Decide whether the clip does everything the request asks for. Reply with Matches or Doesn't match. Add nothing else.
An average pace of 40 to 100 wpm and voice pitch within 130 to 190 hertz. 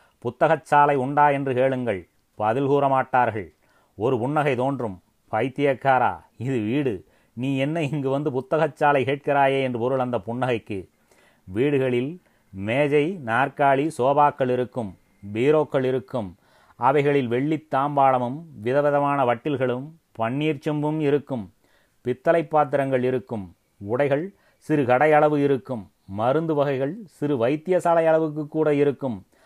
Doesn't match